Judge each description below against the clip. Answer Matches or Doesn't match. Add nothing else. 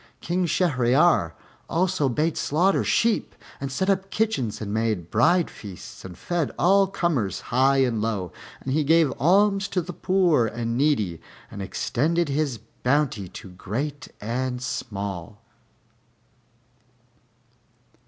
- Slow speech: Matches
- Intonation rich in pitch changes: Matches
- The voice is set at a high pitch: Doesn't match